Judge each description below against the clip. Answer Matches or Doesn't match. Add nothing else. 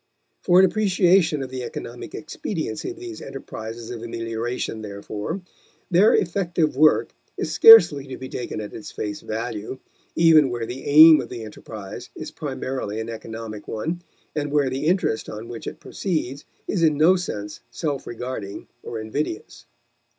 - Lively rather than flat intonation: Matches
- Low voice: Matches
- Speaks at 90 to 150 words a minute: Doesn't match